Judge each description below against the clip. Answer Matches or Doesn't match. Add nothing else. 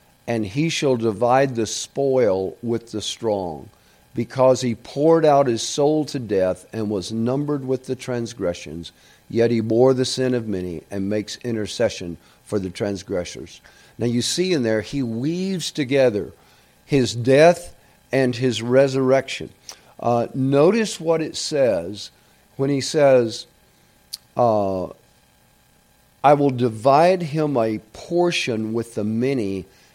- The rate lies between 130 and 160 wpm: Matches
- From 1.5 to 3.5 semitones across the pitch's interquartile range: Doesn't match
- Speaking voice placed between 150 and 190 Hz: Doesn't match